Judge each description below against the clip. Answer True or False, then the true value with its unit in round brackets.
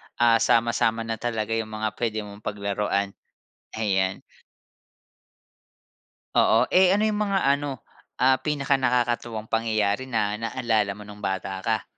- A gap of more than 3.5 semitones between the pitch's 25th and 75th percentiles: False (3.2 semitones)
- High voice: False (115 Hz)